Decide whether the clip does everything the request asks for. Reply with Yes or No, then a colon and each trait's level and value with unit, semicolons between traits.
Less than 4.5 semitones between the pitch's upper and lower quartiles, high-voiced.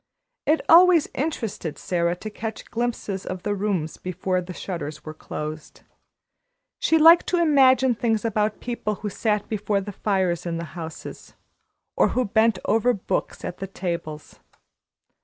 No: average, 5.0 semitones; high, 205 Hz